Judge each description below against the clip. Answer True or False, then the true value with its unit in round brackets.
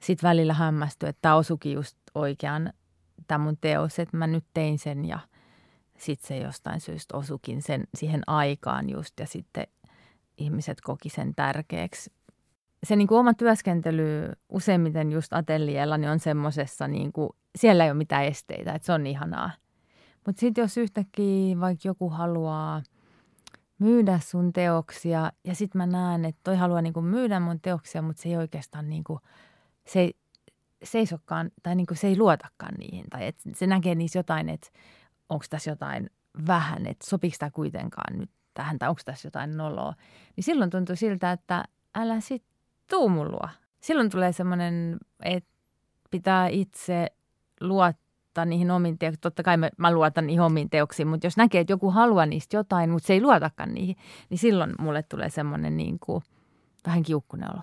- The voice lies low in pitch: False (170 Hz)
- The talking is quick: True (160 wpm)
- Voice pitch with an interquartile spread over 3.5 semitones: False (3.2 semitones)